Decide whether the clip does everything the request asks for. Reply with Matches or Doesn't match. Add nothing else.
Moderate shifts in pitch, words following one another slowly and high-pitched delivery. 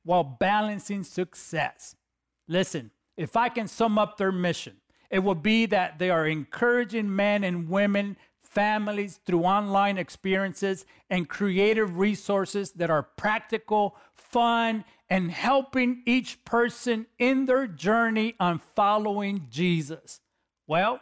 Matches